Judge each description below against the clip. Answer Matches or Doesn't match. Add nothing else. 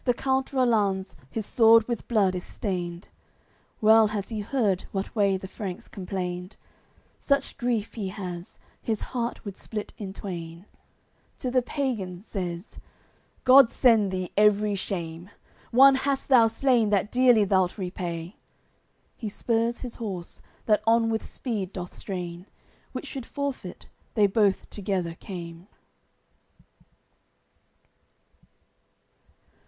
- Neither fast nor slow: Doesn't match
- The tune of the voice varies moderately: Matches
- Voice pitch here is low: Doesn't match